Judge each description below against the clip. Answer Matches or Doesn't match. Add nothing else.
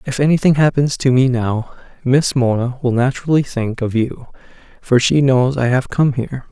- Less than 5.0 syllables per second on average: Doesn't match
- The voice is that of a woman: Doesn't match